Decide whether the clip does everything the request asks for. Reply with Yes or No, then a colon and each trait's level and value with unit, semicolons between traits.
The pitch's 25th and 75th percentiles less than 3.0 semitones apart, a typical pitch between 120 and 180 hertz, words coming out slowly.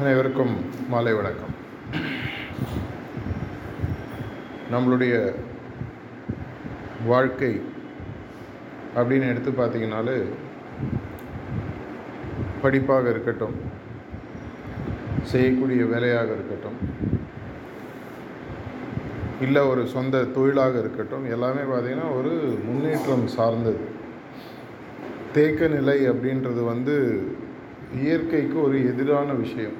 Yes: narrow, 2.4 semitones; low, 125 Hz; slow, 60 wpm